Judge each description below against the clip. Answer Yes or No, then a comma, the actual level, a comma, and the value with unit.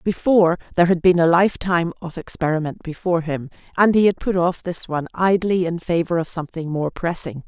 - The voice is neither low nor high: Yes, medium, 170 Hz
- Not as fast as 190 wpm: No, average, 195 wpm